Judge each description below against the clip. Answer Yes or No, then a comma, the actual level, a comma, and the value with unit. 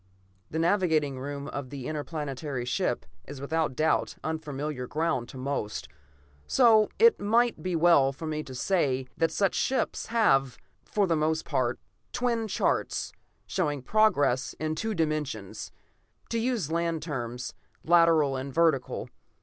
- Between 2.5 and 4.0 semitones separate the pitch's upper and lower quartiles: No, average, 4.6 semitones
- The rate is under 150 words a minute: Yes, average, 140 wpm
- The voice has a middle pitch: Yes, medium, 155 Hz